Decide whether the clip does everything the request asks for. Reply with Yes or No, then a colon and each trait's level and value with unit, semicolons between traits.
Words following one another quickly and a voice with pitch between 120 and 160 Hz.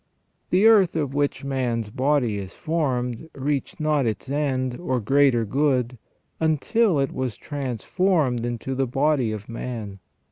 No: average, 140 wpm; low, 135 Hz